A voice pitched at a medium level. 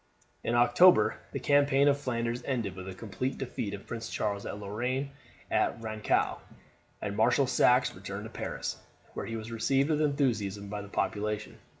No: low, 115 Hz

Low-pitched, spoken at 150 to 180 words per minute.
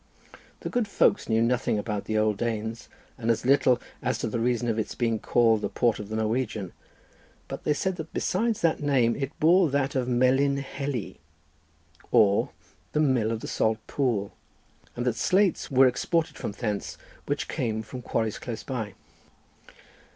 Yes: low, 120 Hz; average, 170 wpm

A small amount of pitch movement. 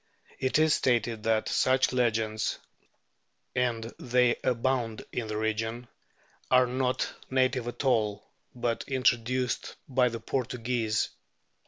Yes: narrow, 2.2 semitones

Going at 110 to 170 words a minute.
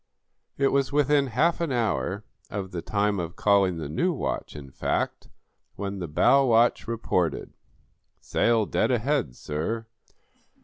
Yes: average, 140 wpm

